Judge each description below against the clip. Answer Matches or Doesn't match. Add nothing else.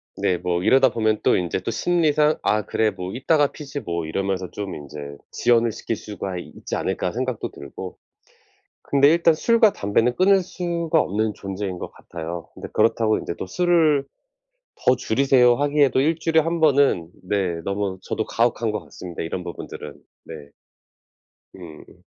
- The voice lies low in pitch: Matches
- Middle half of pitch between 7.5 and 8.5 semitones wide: Matches